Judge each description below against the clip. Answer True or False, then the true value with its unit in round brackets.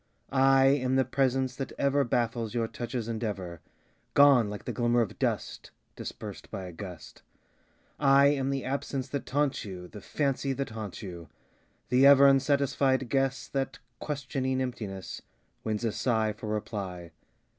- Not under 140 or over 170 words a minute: True (150 wpm)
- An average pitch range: True (4.2 semitones)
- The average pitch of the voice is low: True (125 Hz)